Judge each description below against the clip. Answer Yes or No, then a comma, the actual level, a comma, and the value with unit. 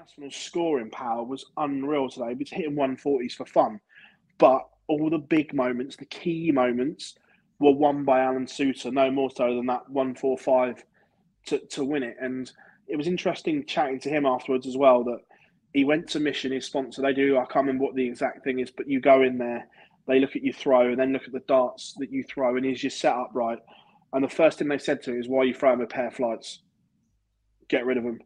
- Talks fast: Yes, fast, 225 wpm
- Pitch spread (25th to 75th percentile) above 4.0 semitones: No, average, 2.9 semitones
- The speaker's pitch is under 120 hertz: No, low, 135 Hz